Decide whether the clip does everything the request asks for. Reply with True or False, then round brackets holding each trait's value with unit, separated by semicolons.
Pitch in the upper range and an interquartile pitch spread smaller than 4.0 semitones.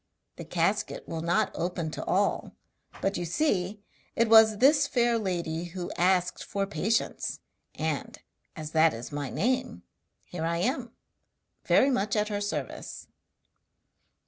False (195 Hz; 4.9 semitones)